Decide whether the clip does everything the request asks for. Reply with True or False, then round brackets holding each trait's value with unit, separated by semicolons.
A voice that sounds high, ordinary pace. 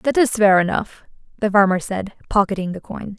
True (200 Hz; 190 wpm)